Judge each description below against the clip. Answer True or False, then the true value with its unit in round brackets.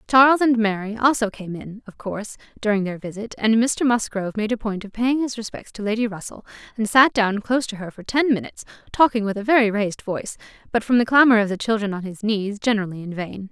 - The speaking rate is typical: False (230 wpm)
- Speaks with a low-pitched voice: False (220 Hz)